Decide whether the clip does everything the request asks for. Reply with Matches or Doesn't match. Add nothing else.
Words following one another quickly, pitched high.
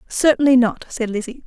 Doesn't match